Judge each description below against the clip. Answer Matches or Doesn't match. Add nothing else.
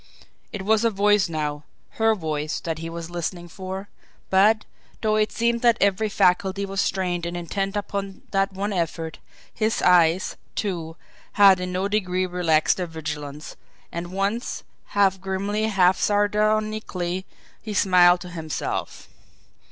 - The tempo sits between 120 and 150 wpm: Matches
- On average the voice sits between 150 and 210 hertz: Matches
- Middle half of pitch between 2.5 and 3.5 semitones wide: Matches